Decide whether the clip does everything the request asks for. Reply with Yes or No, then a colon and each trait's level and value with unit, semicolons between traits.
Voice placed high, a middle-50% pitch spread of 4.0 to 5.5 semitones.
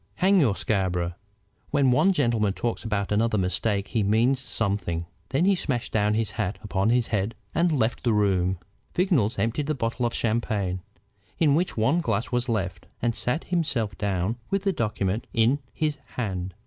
No: low, 115 Hz; average, 5.1 semitones